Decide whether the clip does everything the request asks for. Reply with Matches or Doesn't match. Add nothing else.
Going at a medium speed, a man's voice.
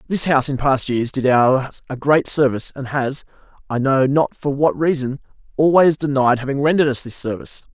Matches